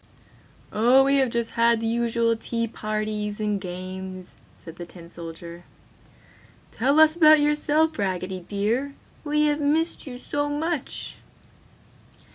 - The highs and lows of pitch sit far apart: Yes, wide, 7.1 semitones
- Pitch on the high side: Yes, high, 230 Hz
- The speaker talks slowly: Yes, slow, 130 wpm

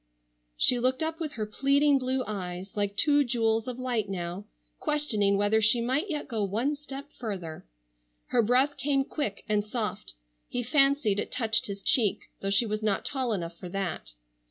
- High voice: Yes, high, 225 Hz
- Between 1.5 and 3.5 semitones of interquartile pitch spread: No, average, 5.2 semitones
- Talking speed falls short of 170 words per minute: No, average, 180 wpm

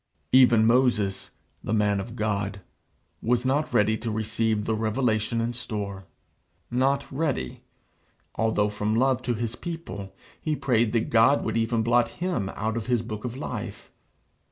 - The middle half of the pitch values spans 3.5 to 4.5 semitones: No, average, 2.7 semitones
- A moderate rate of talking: Yes, average, 155 wpm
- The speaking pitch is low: Yes, low, 115 Hz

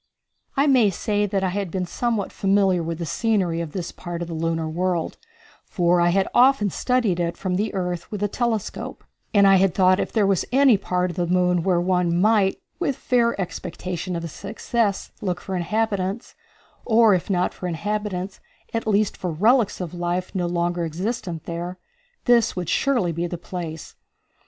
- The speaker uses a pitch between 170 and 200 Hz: Yes, medium, 185 Hz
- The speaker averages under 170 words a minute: No, average, 185 wpm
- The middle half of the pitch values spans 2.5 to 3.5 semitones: Yes, average, 3.2 semitones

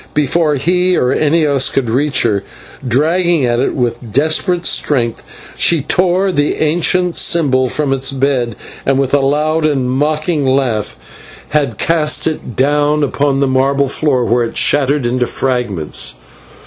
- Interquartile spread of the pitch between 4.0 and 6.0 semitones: No, average, 3.3 semitones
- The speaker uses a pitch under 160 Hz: Yes, medium, 140 Hz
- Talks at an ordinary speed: Yes, average, 155 wpm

